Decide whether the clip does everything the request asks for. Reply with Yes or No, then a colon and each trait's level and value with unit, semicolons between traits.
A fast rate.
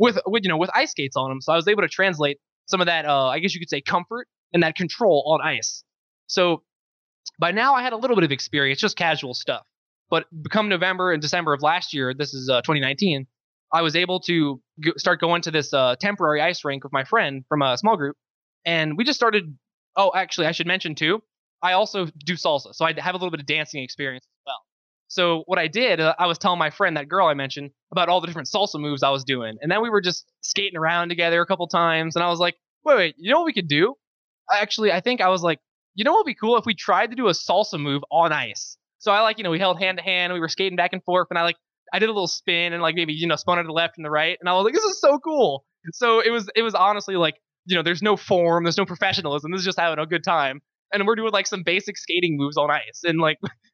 Yes: fast, 275 wpm